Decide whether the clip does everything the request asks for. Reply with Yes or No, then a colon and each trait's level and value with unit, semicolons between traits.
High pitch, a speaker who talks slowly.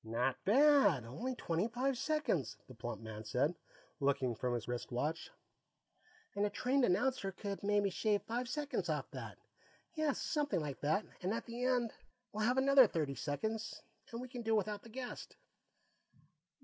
No: high, 210 Hz; average, 170 wpm